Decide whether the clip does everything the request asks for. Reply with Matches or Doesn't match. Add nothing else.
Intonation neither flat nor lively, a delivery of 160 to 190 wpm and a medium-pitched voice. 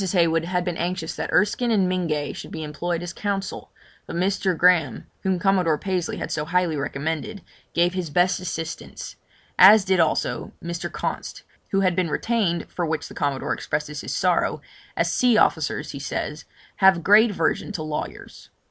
Matches